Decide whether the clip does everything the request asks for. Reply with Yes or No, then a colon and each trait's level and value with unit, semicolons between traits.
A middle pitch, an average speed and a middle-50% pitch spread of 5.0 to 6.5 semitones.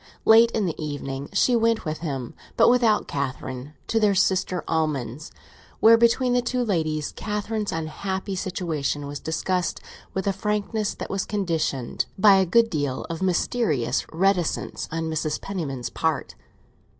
Yes: medium, 180 Hz; average, 150 wpm; wide, 5.6 semitones